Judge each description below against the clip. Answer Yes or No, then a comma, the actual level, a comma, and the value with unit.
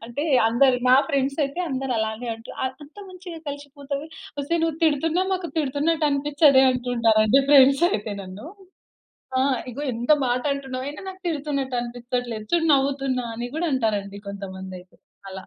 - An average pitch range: Yes, average, 3.7 semitones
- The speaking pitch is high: Yes, very high, 270 Hz